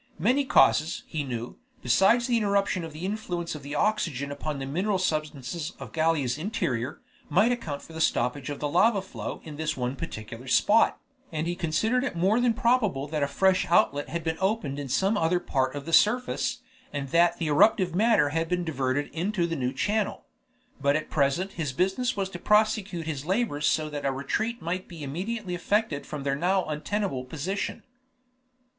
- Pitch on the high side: No, medium, 165 Hz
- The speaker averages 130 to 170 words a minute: No, average, 190 wpm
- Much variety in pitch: Yes, wide, 5.7 semitones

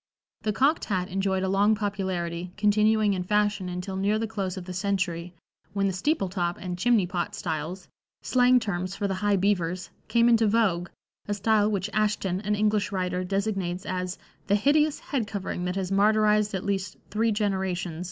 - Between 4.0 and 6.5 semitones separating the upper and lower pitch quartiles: No, narrow, 2.6 semitones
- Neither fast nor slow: Yes, average, 180 wpm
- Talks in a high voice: Yes, high, 195 Hz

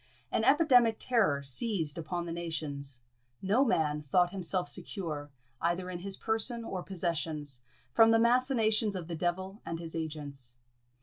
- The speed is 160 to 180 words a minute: No, average, 145 wpm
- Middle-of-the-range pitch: Yes, medium, 175 Hz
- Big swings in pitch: Yes, wide, 5.8 semitones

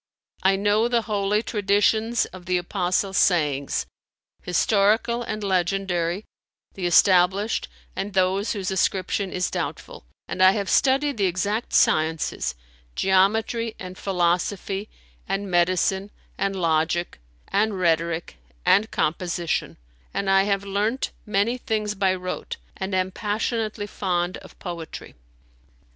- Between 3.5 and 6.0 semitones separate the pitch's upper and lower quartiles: No, narrow, 2.6 semitones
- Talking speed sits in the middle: No, slow, 120 wpm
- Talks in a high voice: Yes, high, 195 Hz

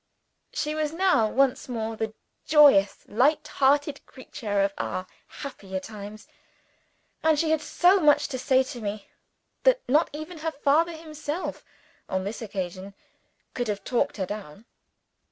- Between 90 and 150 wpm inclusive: Yes, average, 145 wpm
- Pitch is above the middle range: Yes, very high, 260 Hz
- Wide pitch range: Yes, wide, 6.7 semitones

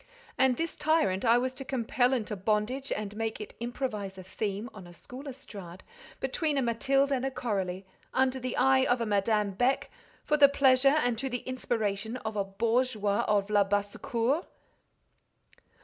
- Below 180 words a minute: Yes, average, 165 wpm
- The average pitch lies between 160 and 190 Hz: No, high, 235 Hz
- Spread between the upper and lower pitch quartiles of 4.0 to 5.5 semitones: Yes, average, 4.3 semitones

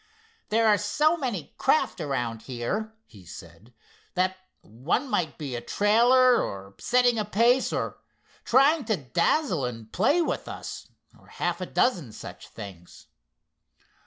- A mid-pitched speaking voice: No, high, 195 Hz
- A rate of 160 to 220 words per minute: No, average, 140 wpm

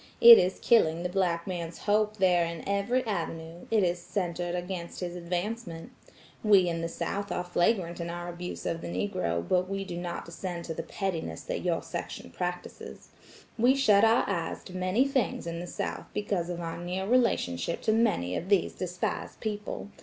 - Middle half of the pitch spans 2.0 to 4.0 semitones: Yes, average, 3.0 semitones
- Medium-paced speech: Yes, average, 185 wpm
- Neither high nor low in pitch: Yes, medium, 180 Hz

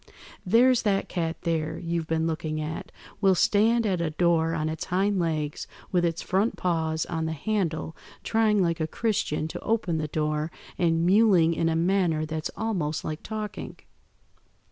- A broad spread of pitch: No, average, 3.6 semitones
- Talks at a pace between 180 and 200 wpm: No, average, 165 wpm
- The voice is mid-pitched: Yes, medium, 170 Hz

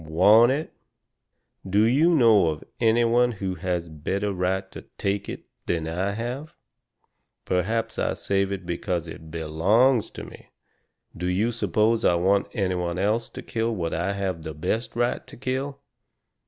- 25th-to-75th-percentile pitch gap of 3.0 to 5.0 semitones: Yes, average, 4.6 semitones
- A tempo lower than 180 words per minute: Yes, average, 170 wpm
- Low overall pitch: Yes, low, 100 Hz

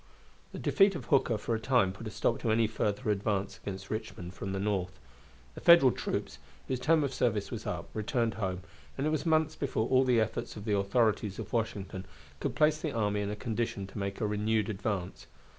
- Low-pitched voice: Yes, low, 110 Hz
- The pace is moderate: No, fast, 210 wpm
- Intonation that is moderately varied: Yes, average, 4.2 semitones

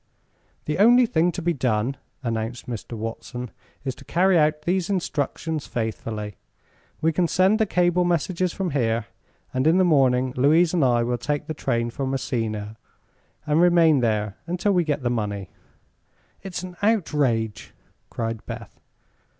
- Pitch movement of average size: No, wide, 6.9 semitones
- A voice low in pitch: No, medium, 145 Hz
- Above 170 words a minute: No, average, 155 wpm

